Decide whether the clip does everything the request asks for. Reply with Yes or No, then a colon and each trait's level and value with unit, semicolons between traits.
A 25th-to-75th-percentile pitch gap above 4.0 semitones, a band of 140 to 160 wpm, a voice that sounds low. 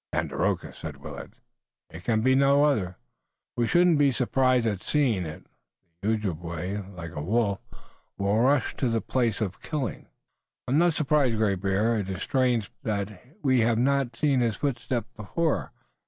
No: average, 5.0 semitones; average, 170 wpm; low, 115 Hz